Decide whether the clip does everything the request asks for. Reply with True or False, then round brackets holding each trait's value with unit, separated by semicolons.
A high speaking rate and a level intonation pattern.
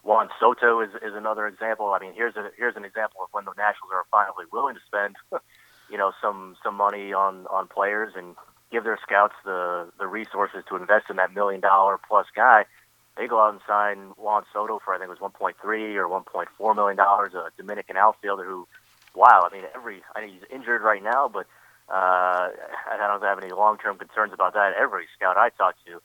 True (220 wpm; 1.7 semitones)